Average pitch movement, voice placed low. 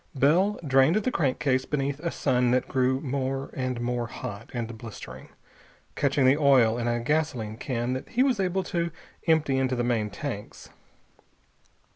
Yes: average, 3.7 semitones; low, 130 Hz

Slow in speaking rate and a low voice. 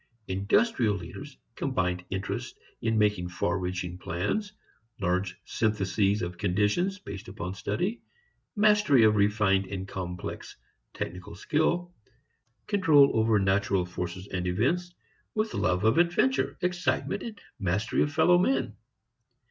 Yes: slow, 120 wpm; low, 105 Hz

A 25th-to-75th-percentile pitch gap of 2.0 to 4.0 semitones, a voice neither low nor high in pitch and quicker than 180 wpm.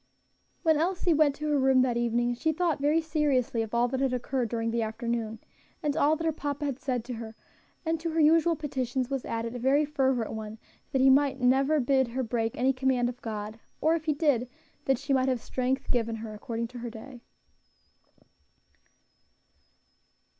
No: average, 3.7 semitones; very high, 260 Hz; average, 195 wpm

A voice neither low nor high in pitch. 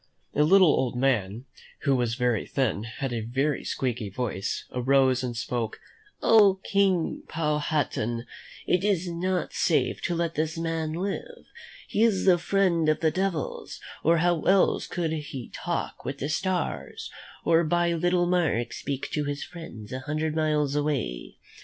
Yes: medium, 155 Hz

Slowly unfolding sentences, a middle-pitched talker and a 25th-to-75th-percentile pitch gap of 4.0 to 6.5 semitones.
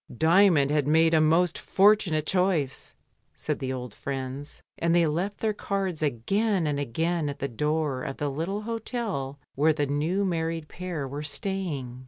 No: average, 165 wpm; medium, 160 Hz; average, 4.5 semitones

